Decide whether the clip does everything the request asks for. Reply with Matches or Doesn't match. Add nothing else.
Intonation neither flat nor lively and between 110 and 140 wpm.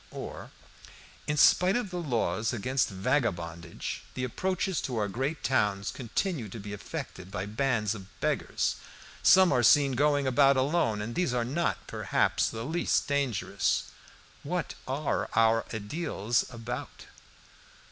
Doesn't match